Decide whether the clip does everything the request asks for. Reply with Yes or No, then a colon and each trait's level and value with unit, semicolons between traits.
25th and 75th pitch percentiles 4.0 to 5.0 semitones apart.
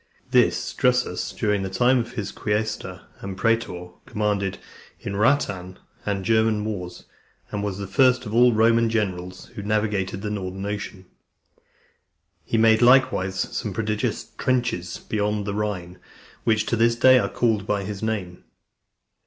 No: average, 2.8 semitones